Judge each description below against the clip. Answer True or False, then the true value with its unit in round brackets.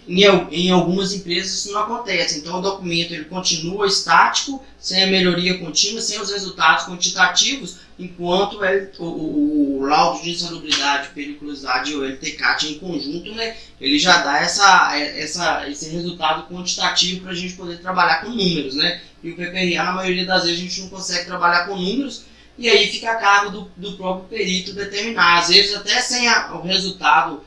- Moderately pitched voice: True (180 Hz)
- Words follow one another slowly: False (180 wpm)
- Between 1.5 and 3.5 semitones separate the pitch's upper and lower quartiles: True (2.9 semitones)